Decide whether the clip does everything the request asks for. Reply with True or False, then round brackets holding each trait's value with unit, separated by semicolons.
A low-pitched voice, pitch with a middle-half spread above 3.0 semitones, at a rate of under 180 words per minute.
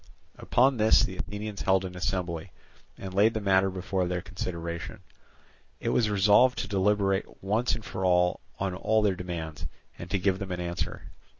False (95 Hz; 2.4 semitones; 170 wpm)